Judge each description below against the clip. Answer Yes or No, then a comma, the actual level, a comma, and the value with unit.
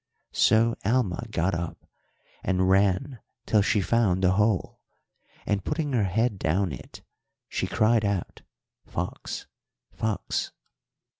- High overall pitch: No, low, 100 Hz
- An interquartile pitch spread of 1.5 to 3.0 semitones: No, average, 3.6 semitones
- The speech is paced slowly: Yes, slow, 120 wpm